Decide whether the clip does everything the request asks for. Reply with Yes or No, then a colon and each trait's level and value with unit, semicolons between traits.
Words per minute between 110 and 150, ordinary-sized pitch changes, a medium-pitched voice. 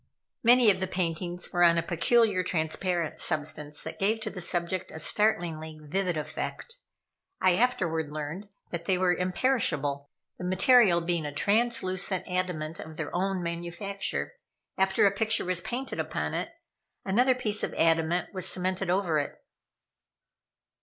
Yes: average, 145 wpm; average, 3.4 semitones; medium, 180 Hz